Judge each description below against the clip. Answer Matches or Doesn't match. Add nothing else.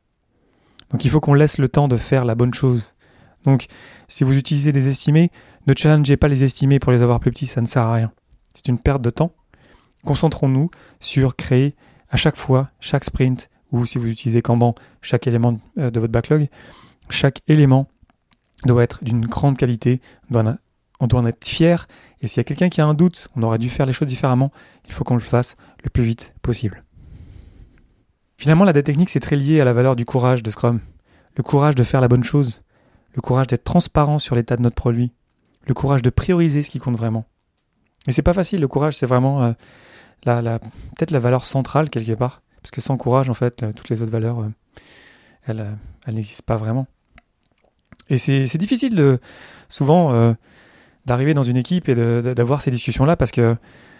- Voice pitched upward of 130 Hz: Doesn't match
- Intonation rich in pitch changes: Doesn't match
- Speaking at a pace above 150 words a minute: Matches